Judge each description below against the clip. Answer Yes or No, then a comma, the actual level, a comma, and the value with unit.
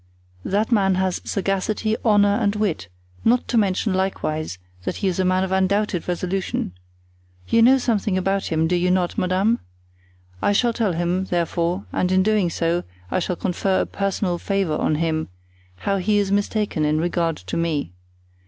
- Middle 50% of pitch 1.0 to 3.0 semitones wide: Yes, average, 2.7 semitones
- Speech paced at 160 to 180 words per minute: Yes, average, 170 wpm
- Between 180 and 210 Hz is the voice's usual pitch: Yes, high, 190 Hz